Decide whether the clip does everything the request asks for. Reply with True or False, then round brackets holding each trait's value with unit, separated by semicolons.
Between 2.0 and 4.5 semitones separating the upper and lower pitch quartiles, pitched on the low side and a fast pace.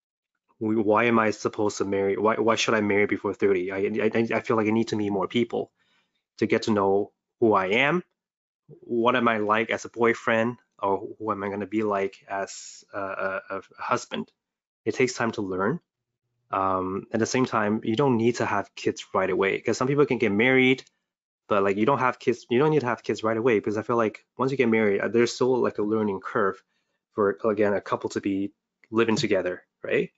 True (2.6 semitones; 110 Hz; 225 wpm)